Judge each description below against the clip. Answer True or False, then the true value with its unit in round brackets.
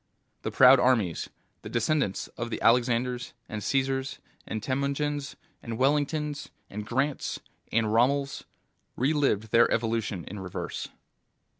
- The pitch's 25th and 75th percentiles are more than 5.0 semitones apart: False (3.7 semitones)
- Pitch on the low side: True (125 Hz)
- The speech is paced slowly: True (120 wpm)